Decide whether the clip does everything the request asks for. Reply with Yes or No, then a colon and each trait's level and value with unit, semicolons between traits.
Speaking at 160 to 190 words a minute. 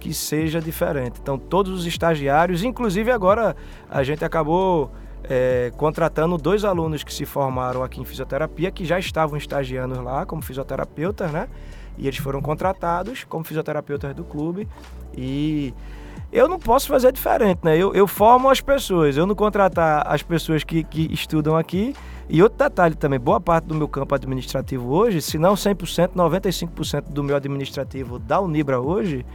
Yes: average, 165 wpm